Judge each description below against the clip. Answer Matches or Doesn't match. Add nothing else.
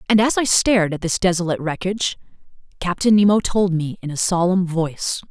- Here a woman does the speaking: Matches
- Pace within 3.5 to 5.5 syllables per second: Doesn't match